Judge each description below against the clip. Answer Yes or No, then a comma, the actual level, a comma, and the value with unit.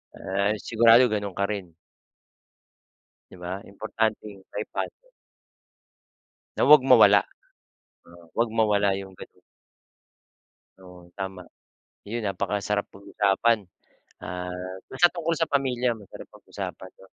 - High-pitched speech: No, low, 105 Hz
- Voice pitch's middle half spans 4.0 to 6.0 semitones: No, average, 3.3 semitones